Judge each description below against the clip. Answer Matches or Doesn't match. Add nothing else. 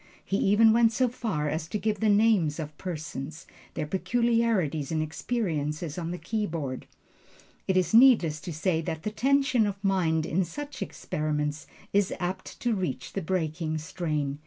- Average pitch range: Doesn't match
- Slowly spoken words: Doesn't match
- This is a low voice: Doesn't match